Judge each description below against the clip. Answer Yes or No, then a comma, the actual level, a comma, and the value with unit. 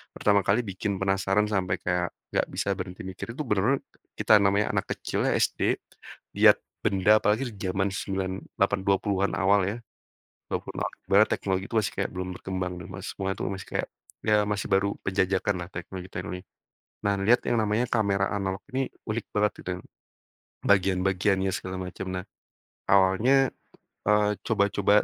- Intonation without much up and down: Yes, narrow, 1.6 semitones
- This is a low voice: Yes, very low, 95 Hz